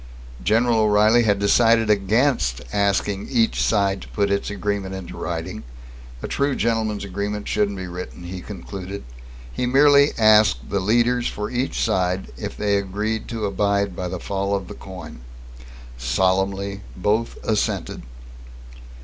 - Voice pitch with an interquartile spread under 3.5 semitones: Yes, narrow, 2.4 semitones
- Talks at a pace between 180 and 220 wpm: No, average, 140 wpm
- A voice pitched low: Yes, low, 100 Hz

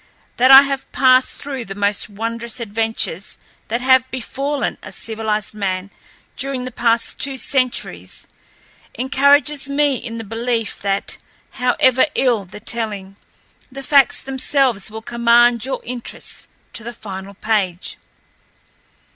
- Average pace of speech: No, slow, 130 wpm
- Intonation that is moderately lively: Yes, average, 3.6 semitones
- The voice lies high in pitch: Yes, high, 235 Hz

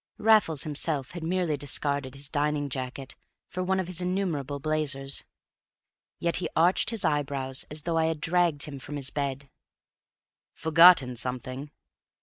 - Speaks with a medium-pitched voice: Yes, medium, 150 Hz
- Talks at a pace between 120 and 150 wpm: Yes, average, 145 wpm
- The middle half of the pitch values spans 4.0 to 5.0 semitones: No, average, 3.6 semitones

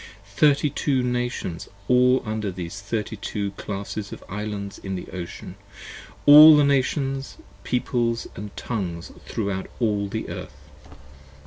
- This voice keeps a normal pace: No, slow, 125 wpm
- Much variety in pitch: No, average, 4.1 semitones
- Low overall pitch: Yes, low, 110 Hz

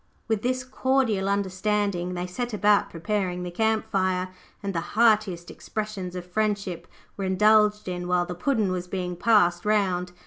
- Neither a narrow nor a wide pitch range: Yes, average, 3.0 semitones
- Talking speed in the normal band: Yes, average, 160 wpm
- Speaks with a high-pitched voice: Yes, high, 195 Hz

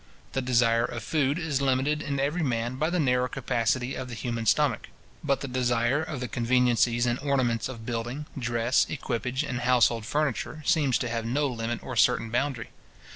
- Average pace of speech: Yes, average, 180 wpm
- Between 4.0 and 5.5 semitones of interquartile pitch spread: No, average, 2.9 semitones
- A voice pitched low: Yes, low, 125 Hz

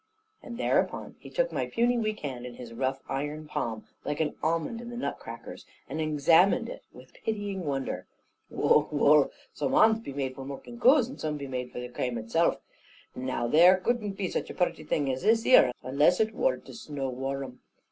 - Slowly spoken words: No, average, 200 wpm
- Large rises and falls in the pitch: Yes, wide, 8.3 semitones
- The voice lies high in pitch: No, medium, 150 Hz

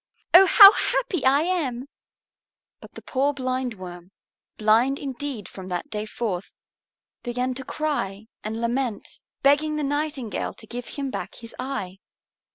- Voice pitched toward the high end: Yes, very high, 255 Hz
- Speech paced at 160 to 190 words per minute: No, average, 140 wpm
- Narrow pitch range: No, average, 4.8 semitones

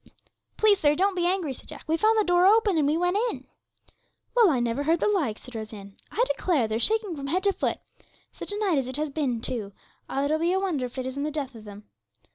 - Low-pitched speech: No, very high, 310 Hz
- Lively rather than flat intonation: Yes, wide, 6.9 semitones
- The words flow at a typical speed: No, fast, 255 wpm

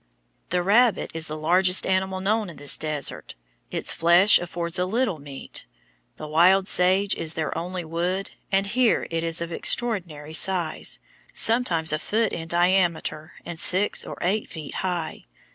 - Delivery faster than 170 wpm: No, average, 160 wpm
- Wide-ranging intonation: No, average, 2.9 semitones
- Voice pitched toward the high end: No, medium, 175 Hz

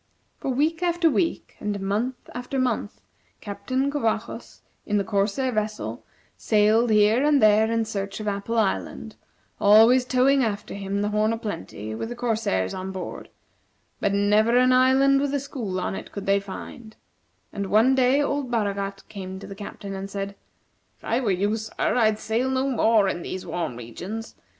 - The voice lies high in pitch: Yes, high, 215 Hz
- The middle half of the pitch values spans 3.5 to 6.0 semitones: Yes, average, 4.1 semitones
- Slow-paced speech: No, average, 175 wpm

